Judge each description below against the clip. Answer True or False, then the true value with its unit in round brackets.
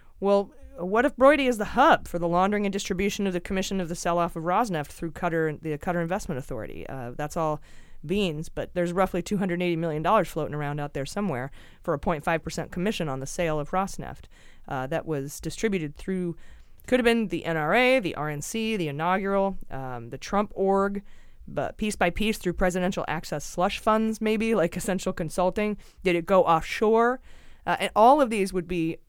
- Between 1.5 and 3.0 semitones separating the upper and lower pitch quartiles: False (3.8 semitones)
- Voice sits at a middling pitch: True (180 Hz)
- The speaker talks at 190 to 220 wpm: True (195 wpm)